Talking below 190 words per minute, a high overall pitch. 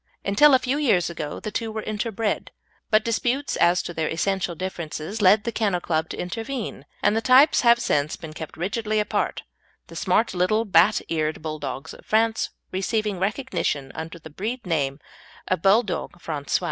Yes: average, 170 wpm; high, 195 Hz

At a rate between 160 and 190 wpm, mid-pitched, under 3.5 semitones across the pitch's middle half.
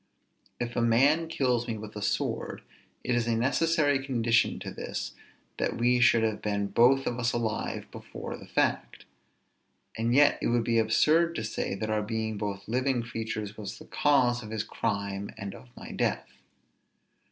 No: average, 175 wpm; low, 115 Hz; narrow, 2.6 semitones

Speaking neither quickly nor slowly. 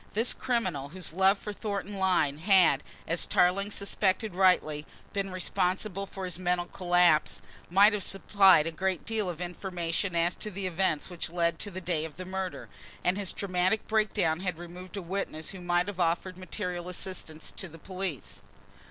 Yes: average, 180 wpm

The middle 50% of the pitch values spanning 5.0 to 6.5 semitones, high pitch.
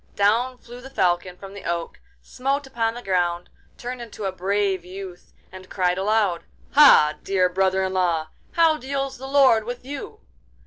Yes: wide, 5.6 semitones; high, 200 Hz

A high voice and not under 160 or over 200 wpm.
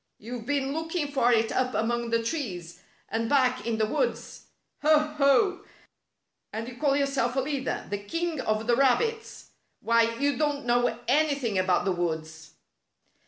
Yes: very high, 250 Hz; average, 165 wpm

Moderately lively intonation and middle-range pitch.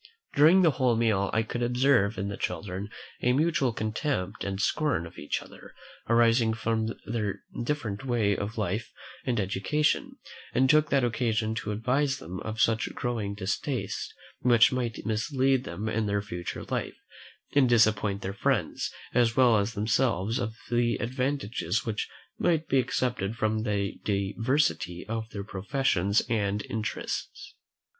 No: average, 3.7 semitones; low, 110 Hz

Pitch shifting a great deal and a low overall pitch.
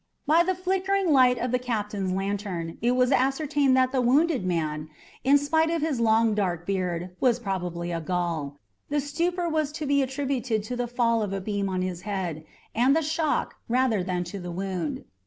No: wide, 7.4 semitones; high, 230 Hz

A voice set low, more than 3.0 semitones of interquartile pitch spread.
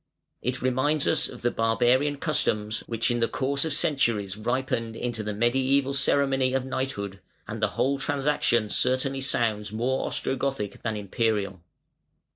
Yes: low, 125 Hz; average, 3.4 semitones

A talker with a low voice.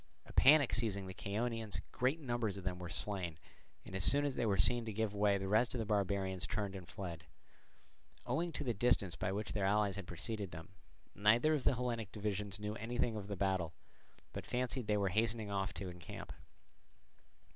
Yes: low, 105 Hz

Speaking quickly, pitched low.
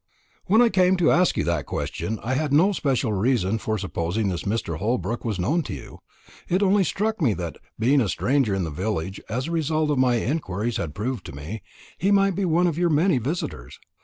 Yes: fast, 220 wpm; low, 125 Hz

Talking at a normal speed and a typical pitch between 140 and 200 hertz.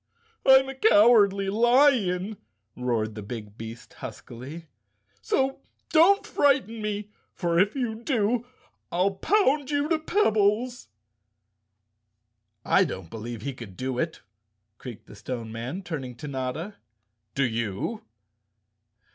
No: slow, 120 wpm; medium, 185 Hz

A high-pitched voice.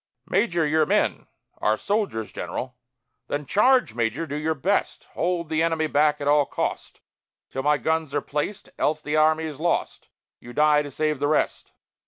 No: medium, 150 Hz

